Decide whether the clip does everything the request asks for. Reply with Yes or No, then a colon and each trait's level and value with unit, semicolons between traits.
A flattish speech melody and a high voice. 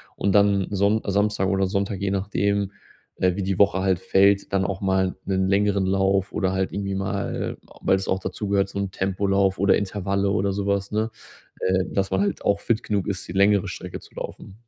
No: narrow, 1.0 semitones; low, 100 Hz